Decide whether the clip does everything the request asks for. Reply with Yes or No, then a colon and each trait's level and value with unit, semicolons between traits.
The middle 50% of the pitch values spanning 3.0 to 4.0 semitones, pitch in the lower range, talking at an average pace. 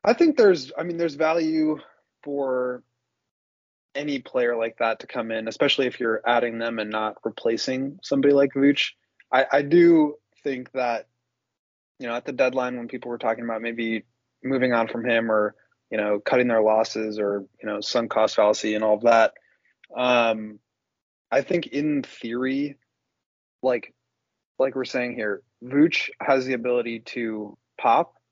Yes: average, 3.5 semitones; low, 125 Hz; average, 165 wpm